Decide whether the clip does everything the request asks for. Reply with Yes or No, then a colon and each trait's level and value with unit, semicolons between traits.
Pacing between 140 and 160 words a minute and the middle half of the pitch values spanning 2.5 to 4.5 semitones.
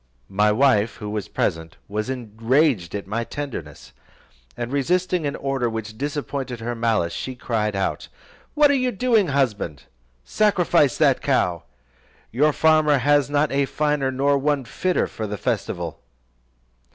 No: average, 145 wpm; average, 5.3 semitones